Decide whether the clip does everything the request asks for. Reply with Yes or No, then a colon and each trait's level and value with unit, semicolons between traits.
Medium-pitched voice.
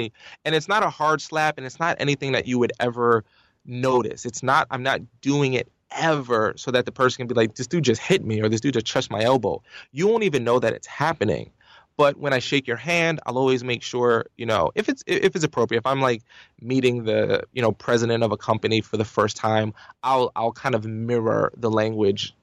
No: low, 125 Hz